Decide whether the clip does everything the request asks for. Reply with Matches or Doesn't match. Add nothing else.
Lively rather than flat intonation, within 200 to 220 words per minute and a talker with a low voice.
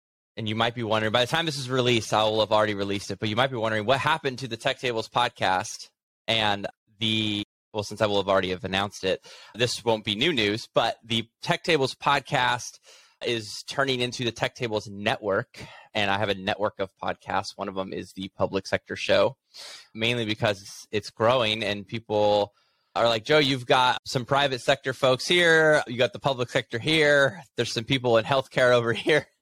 Doesn't match